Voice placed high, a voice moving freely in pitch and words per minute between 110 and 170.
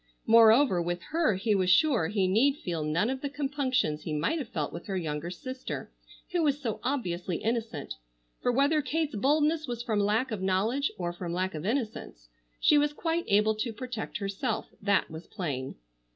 No: high, 220 Hz; wide, 7.4 semitones; average, 185 wpm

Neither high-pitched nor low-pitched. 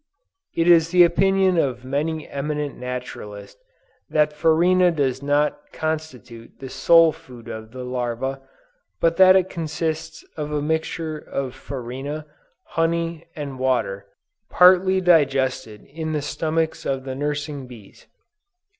Yes: medium, 150 Hz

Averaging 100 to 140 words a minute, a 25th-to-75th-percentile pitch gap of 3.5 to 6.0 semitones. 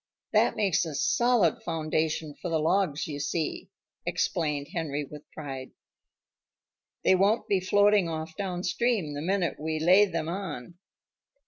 Yes: slow, 135 wpm; average, 3.9 semitones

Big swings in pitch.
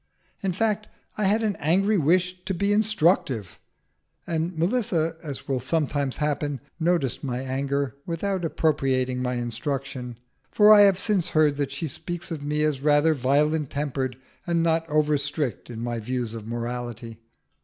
No: average, 4.9 semitones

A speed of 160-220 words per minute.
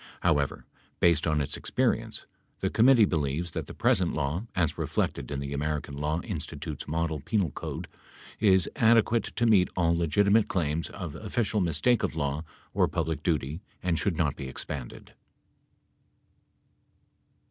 No: average, 145 wpm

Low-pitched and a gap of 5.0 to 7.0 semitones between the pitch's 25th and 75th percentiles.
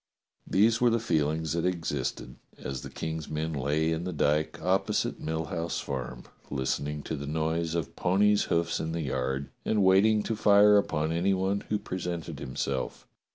No: very low, 80 Hz; average, 4.3 semitones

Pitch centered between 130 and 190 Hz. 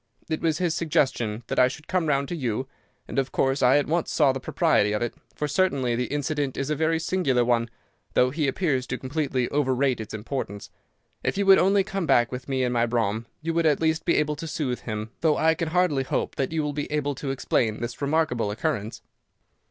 Yes: medium, 140 Hz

